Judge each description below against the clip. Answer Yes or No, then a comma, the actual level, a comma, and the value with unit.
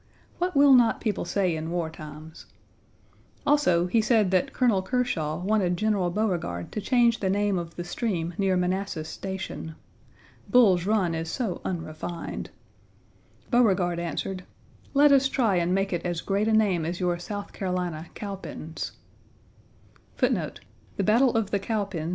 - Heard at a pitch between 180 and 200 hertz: Yes, medium, 185 Hz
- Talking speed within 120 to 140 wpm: Yes, slow, 135 wpm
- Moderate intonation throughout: Yes, average, 4.0 semitones